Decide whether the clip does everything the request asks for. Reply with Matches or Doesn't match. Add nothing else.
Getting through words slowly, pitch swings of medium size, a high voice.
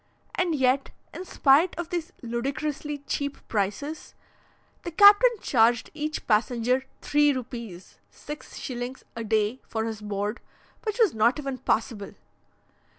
Matches